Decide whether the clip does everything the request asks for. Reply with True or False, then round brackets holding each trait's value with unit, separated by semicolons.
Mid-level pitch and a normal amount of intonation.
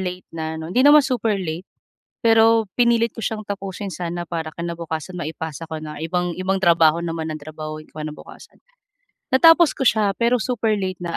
False (180 Hz; 5.7 semitones)